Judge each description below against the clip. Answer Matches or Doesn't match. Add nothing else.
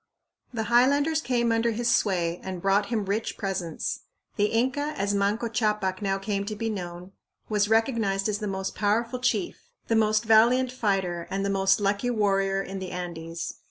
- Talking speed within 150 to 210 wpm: Matches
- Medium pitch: Doesn't match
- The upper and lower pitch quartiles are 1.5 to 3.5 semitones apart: Matches